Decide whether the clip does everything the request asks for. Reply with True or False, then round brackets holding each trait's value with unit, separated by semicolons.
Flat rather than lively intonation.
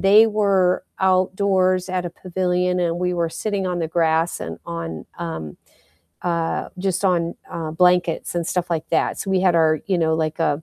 True (2.3 semitones)